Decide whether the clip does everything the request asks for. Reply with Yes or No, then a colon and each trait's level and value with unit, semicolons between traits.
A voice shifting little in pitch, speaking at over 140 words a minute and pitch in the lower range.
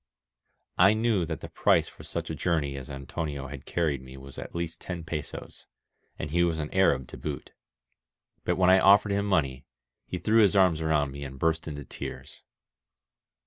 No: average, 4.8 semitones; average, 185 wpm; very low, 80 Hz